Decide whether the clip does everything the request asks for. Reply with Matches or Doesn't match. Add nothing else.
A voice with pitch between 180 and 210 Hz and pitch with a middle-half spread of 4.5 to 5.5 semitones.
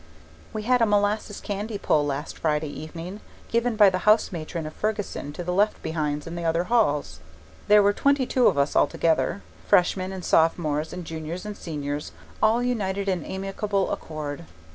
Matches